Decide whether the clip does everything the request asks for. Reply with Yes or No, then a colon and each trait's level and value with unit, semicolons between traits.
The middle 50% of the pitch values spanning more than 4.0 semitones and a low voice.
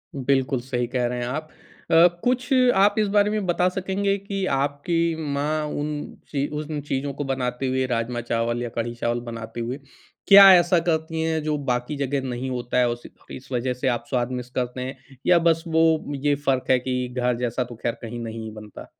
Yes: average, 4.7 semitones; low, 130 Hz